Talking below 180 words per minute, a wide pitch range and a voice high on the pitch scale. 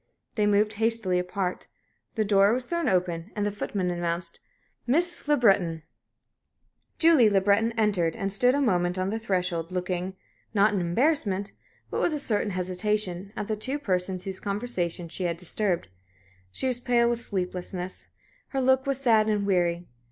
No: average, 165 wpm; average, 4.1 semitones; high, 200 Hz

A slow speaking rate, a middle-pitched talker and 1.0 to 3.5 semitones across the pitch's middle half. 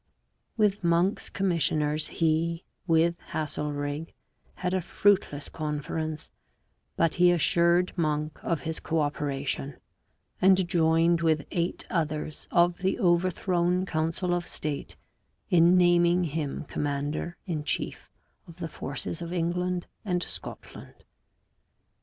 Yes: slow, 115 wpm; medium, 170 Hz; narrow, 2.5 semitones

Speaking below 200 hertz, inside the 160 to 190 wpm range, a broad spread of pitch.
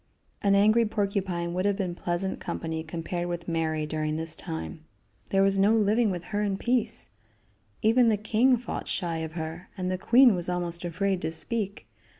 No: medium, 185 Hz; average, 180 wpm; average, 3.7 semitones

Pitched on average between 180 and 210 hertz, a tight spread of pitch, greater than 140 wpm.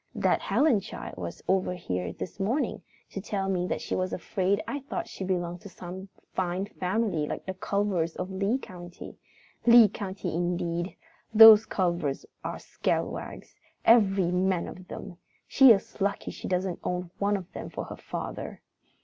Yes: medium, 185 Hz; narrow, 2.3 semitones; average, 165 wpm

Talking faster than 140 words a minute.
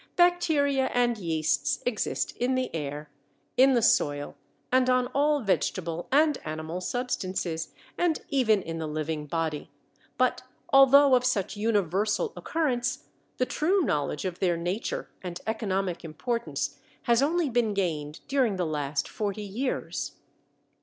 No: slow, 135 wpm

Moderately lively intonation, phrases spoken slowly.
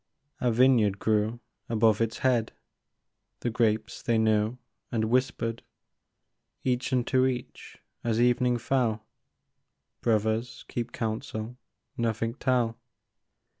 No: narrow, 2.0 semitones; slow, 100 wpm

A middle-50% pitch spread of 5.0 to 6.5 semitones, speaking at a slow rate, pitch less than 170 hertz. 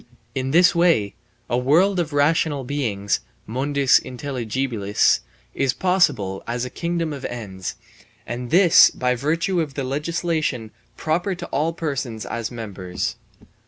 Yes: wide, 5.6 semitones; slow, 130 wpm; low, 135 Hz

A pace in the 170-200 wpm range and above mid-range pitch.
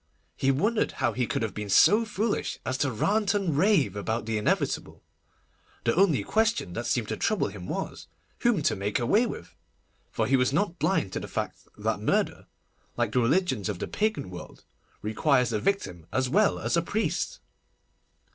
No: average, 185 wpm; low, 130 Hz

